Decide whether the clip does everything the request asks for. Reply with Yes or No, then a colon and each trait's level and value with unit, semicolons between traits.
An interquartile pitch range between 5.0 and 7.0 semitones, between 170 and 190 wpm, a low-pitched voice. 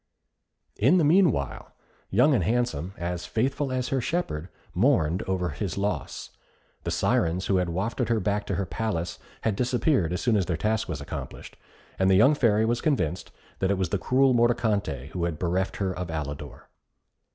Yes: wide, 5.6 semitones; average, 180 wpm; low, 100 Hz